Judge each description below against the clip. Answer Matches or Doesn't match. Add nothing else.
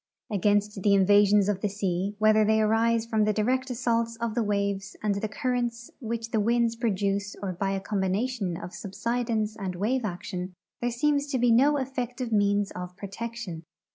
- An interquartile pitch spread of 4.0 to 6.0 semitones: Doesn't match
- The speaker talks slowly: Doesn't match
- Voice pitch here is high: Matches